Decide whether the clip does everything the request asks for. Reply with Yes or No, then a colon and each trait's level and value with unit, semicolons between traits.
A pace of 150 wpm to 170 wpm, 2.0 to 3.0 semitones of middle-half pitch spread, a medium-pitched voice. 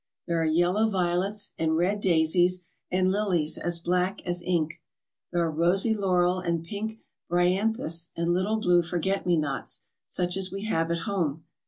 Yes: average, 165 wpm; narrow, 2.4 semitones; medium, 180 Hz